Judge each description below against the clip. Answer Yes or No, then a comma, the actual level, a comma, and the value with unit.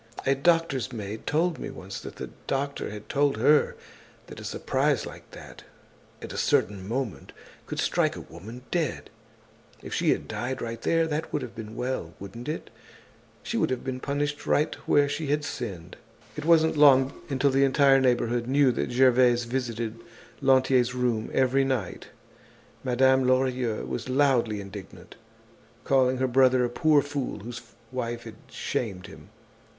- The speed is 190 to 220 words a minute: No, average, 160 wpm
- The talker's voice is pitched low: Yes, low, 130 Hz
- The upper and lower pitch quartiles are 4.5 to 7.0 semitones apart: No, average, 3.0 semitones